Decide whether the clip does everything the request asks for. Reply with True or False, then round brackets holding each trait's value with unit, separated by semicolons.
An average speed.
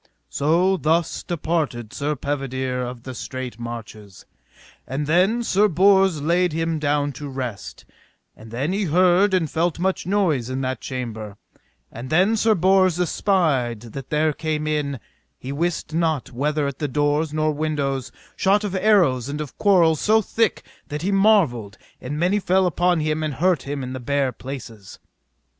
True (165 wpm)